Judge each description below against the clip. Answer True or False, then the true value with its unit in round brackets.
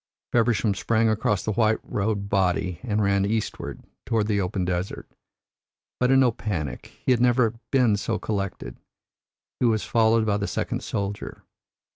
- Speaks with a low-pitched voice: True (105 Hz)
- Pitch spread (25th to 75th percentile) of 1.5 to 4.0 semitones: True (2.5 semitones)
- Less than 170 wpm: True (155 wpm)